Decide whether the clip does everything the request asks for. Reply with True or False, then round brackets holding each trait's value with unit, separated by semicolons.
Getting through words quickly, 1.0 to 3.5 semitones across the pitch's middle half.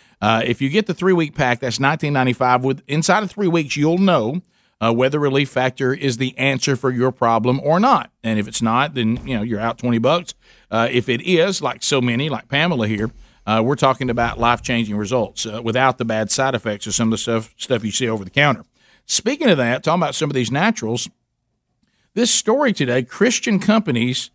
False (210 wpm; 5.0 semitones)